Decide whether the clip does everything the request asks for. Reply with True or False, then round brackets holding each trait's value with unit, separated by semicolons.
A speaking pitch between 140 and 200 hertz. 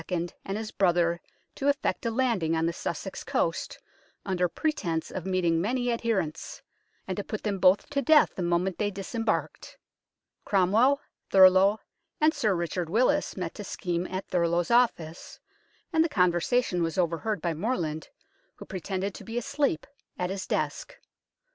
True (190 Hz)